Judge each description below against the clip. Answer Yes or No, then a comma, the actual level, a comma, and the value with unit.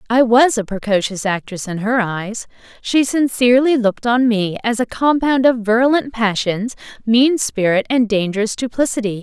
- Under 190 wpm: Yes, average, 155 wpm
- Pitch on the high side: Yes, high, 230 Hz